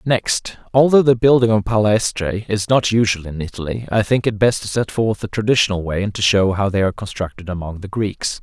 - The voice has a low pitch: Yes, low, 105 Hz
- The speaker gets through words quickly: Yes, fast, 220 wpm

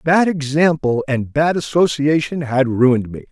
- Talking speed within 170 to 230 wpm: No, average, 145 wpm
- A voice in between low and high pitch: Yes, medium, 145 Hz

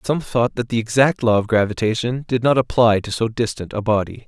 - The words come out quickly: Yes, fast, 225 wpm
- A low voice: Yes, low, 115 Hz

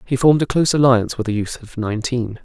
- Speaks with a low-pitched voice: Yes, low, 125 Hz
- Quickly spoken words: Yes, fast, 245 wpm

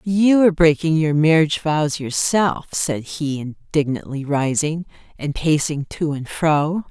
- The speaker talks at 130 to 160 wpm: Yes, average, 140 wpm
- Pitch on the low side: No, medium, 155 Hz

